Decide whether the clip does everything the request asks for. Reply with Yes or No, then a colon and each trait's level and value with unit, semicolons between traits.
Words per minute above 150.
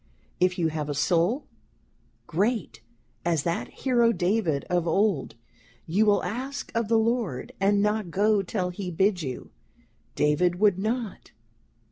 No: average, 140 wpm